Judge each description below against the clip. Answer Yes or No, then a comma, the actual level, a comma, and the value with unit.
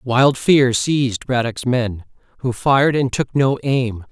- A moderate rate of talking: Yes, average, 175 wpm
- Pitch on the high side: No, low, 125 Hz